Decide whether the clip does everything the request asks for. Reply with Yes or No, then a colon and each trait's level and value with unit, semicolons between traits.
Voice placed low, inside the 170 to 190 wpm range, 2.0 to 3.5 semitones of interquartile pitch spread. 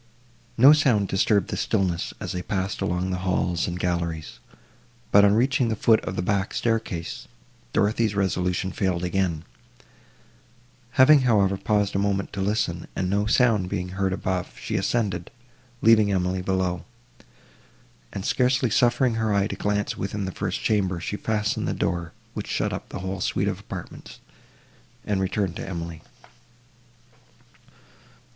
No: low, 100 Hz; average, 150 wpm; average, 2.7 semitones